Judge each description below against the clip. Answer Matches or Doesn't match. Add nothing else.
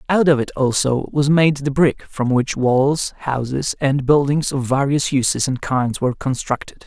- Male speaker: Matches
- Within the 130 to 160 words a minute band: Doesn't match